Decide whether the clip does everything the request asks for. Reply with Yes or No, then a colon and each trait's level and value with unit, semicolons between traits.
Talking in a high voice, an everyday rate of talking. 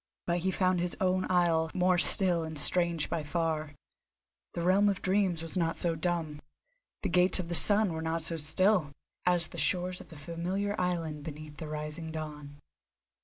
No: medium, 170 Hz; average, 180 wpm